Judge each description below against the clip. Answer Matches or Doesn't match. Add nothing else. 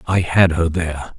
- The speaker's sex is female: Doesn't match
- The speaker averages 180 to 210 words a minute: Matches